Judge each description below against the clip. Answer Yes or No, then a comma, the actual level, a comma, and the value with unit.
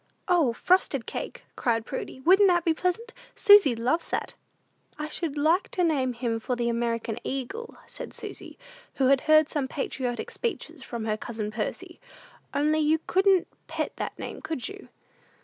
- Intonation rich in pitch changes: Yes, wide, 6.5 semitones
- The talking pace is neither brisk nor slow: Yes, average, 165 wpm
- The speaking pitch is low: No, very high, 290 Hz